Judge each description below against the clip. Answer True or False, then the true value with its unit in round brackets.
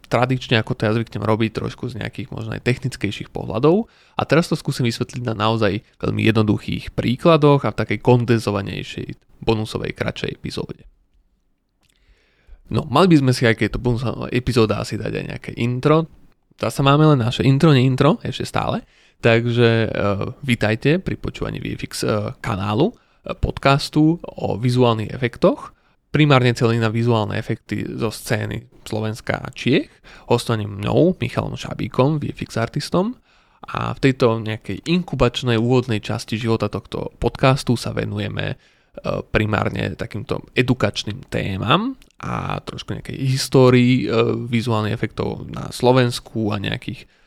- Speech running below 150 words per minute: True (140 wpm)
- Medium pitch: False (120 Hz)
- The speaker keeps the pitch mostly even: False (3.8 semitones)